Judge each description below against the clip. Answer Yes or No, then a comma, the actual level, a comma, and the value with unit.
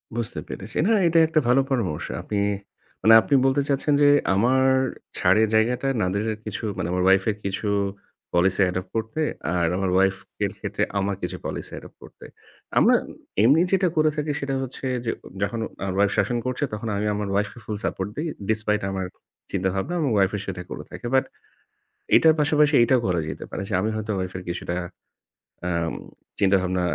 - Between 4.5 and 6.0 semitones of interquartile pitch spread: Yes, wide, 5.6 semitones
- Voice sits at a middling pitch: No, low, 105 Hz